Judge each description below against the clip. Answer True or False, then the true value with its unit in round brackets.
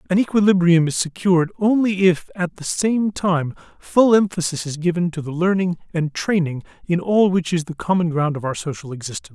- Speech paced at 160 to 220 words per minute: True (195 wpm)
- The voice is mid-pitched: True (175 Hz)